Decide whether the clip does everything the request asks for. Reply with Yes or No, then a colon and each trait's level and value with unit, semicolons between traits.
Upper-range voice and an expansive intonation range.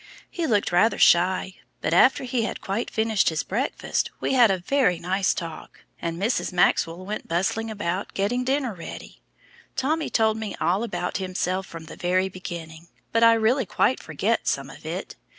No: high, 195 Hz; average, 4.4 semitones